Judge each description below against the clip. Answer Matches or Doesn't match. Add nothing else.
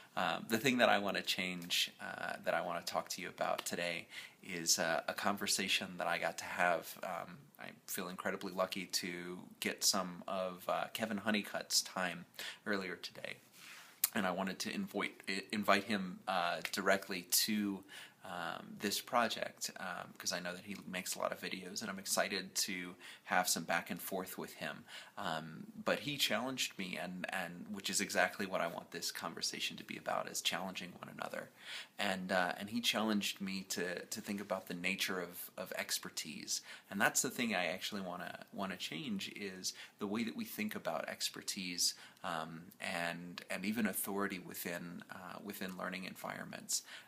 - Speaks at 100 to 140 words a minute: Doesn't match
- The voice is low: Matches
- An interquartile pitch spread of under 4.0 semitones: Matches